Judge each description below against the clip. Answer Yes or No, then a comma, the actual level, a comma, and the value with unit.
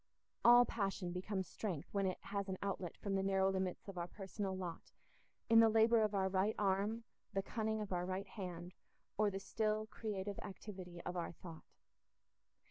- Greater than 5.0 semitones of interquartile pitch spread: No, narrow, 2.4 semitones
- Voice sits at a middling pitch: No, high, 195 Hz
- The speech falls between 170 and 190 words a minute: Yes, average, 180 wpm